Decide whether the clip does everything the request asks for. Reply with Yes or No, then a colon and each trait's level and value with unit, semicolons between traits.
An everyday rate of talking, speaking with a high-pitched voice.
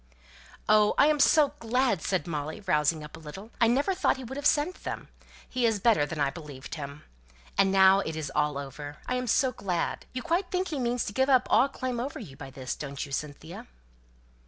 No: fast, 220 wpm; high, 200 Hz